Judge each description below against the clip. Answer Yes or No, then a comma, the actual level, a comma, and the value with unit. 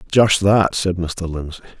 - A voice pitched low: Yes, very low, 90 Hz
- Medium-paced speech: Yes, average, 165 wpm